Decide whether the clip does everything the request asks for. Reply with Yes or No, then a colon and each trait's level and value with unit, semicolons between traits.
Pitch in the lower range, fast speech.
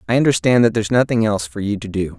Yes: low, 115 Hz; fast, 275 wpm